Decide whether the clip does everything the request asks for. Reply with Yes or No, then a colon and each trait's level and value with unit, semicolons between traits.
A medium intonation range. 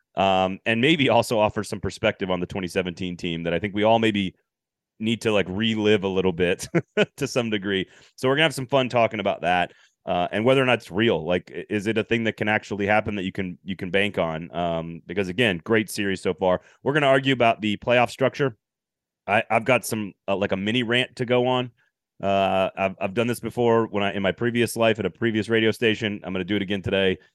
Yes: average, 3.4 semitones